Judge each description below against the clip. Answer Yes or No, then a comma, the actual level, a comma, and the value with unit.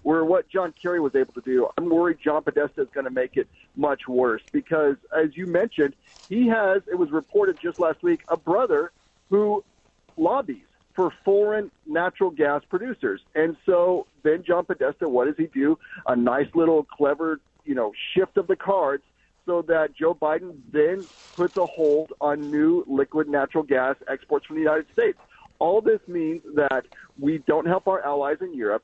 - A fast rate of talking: No, average, 185 wpm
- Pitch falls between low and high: Yes, medium, 175 Hz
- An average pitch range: No, wide, 6.7 semitones